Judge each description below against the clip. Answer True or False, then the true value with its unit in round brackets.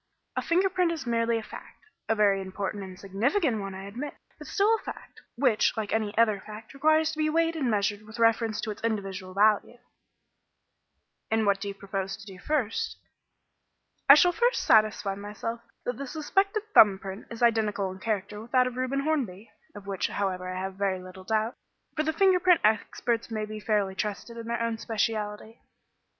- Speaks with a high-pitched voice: True (220 Hz)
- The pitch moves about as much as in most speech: True (4.2 semitones)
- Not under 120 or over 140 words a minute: False (190 wpm)